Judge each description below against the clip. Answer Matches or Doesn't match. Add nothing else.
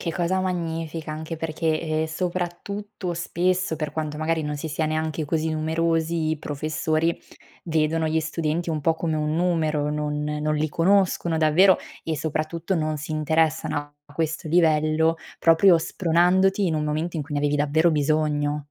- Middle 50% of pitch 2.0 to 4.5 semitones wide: Doesn't match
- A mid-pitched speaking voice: Matches